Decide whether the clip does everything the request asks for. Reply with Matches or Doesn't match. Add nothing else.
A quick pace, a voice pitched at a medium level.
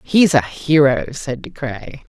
Doesn't match